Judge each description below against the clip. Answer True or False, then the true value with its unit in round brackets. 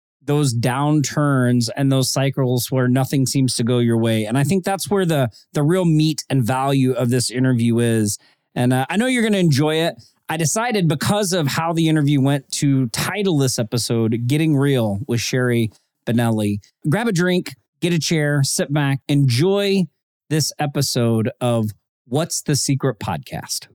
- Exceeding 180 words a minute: False (170 wpm)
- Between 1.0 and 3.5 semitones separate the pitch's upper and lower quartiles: False (4.4 semitones)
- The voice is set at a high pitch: False (135 Hz)